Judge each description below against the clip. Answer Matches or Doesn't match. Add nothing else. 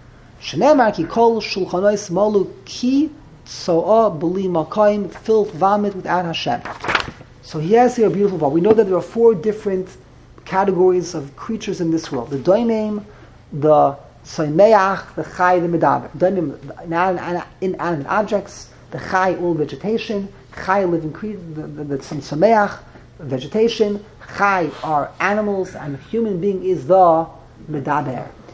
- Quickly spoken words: Doesn't match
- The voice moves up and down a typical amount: Matches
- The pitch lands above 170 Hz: Matches